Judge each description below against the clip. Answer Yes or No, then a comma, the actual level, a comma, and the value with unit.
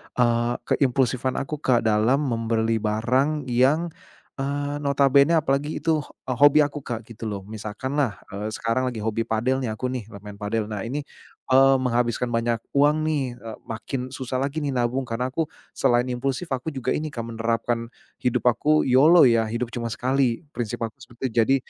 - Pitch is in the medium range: No, low, 125 Hz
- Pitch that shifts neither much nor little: Yes, average, 3.3 semitones